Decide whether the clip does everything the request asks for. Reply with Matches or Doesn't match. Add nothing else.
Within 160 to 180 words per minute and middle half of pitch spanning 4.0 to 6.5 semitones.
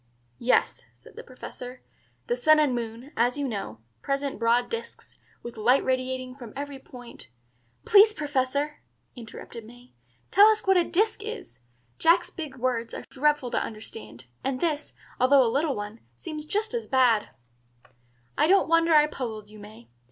Matches